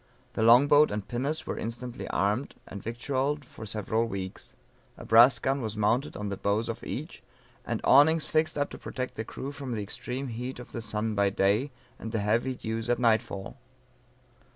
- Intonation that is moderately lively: Yes, average, 3.7 semitones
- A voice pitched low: Yes, low, 115 Hz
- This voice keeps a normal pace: Yes, average, 190 wpm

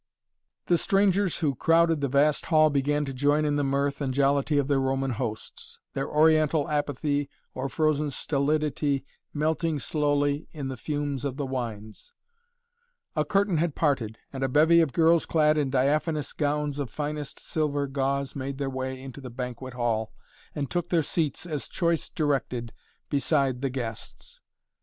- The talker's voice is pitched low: No, medium, 145 Hz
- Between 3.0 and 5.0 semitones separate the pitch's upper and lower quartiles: No, narrow, 2.4 semitones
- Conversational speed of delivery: Yes, average, 160 wpm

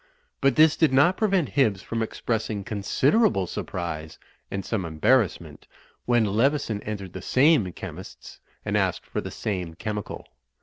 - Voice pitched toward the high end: No, low, 110 Hz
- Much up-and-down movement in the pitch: Yes, wide, 6.3 semitones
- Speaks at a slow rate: No, average, 145 wpm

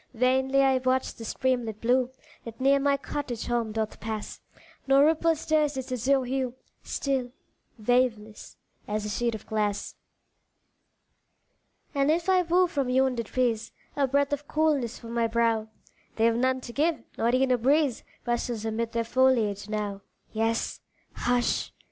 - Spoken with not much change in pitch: No, average, 3.3 semitones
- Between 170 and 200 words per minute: No, average, 150 wpm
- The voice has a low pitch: No, very high, 250 Hz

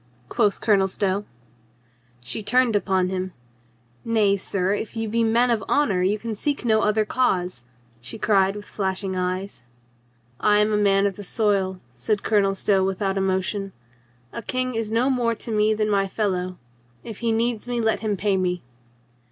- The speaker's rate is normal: Yes, average, 180 wpm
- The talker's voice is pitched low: No, high, 205 Hz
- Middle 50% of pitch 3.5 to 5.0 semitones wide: No, average, 2.7 semitones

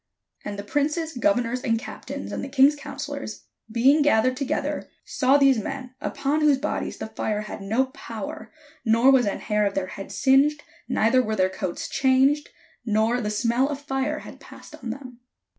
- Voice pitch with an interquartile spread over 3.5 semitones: Yes, average, 4.2 semitones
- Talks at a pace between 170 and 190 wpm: Yes, average, 175 wpm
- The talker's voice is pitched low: No, very high, 255 Hz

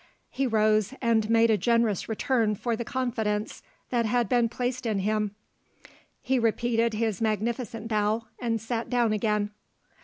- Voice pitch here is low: No, high, 225 Hz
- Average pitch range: No, narrow, 1.8 semitones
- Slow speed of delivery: No, average, 150 wpm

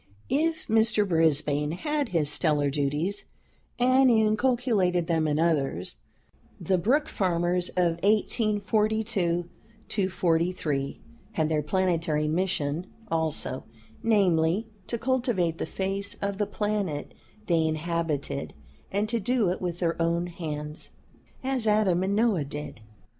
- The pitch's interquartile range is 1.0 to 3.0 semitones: No, average, 5.0 semitones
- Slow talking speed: Yes, slow, 120 wpm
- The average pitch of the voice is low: No, medium, 180 Hz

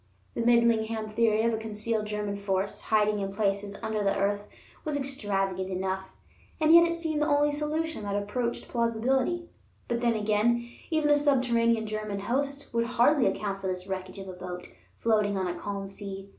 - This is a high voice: Yes, high, 220 Hz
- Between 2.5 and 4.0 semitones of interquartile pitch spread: Yes, average, 3.7 semitones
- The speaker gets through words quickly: No, average, 180 wpm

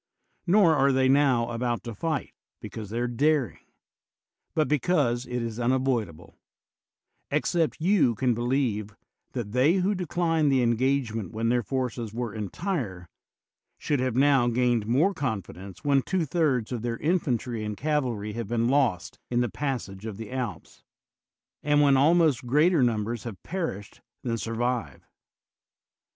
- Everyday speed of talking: Yes, average, 150 wpm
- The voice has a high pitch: No, low, 125 Hz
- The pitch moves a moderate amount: Yes, average, 4.2 semitones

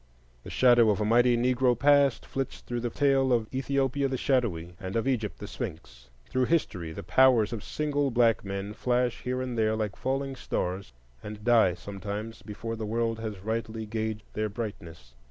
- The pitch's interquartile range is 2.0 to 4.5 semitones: Yes, average, 3.4 semitones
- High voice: No, low, 115 Hz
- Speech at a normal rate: Yes, average, 180 wpm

